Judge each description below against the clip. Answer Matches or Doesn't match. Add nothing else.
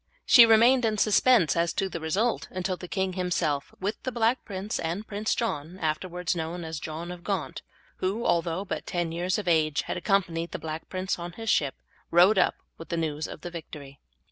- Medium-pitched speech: Matches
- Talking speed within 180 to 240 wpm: Matches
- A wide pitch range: Doesn't match